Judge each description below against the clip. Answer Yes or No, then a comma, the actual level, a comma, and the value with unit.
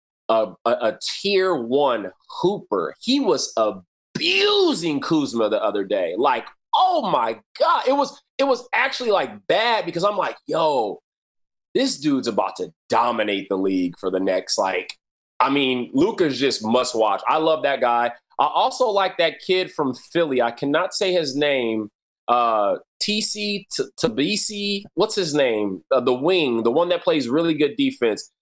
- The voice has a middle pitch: Yes, medium, 175 Hz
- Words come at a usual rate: Yes, average, 165 wpm